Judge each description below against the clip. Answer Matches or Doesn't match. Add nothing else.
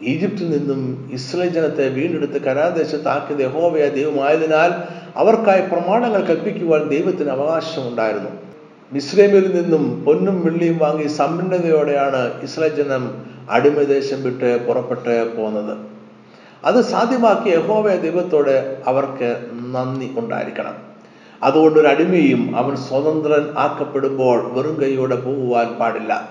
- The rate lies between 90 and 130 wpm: Matches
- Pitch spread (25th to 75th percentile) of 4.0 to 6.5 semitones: Matches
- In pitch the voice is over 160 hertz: Doesn't match